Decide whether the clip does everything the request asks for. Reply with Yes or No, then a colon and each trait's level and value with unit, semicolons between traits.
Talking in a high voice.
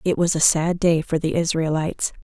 No: medium, 165 Hz